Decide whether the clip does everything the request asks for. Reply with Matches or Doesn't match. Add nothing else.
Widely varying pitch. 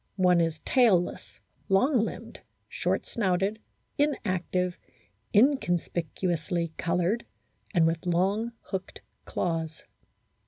Doesn't match